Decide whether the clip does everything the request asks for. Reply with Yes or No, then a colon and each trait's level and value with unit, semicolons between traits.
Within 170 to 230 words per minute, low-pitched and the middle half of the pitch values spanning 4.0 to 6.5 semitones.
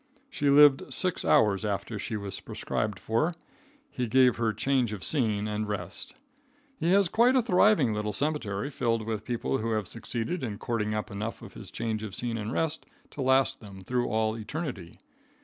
Yes: average, 185 wpm; low, 115 Hz; average, 4.3 semitones